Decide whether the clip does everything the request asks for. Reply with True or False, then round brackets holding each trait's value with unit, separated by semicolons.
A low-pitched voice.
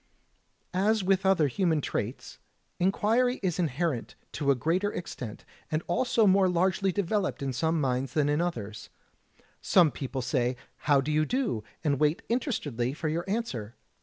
False (165 Hz)